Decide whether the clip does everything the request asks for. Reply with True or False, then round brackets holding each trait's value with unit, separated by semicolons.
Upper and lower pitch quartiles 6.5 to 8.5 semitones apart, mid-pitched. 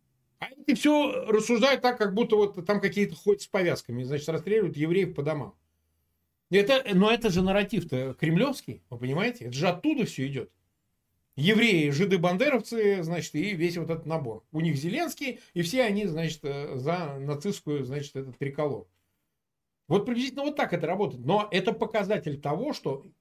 True (6.8 semitones; 175 Hz)